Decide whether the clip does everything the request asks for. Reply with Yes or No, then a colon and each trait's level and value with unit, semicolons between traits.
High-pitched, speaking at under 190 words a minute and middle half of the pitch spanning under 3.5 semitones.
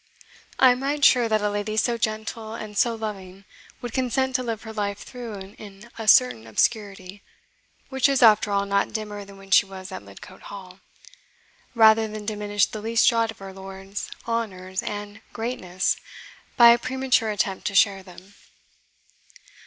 Yes: high, 210 Hz; average, 170 wpm; average, 2.8 semitones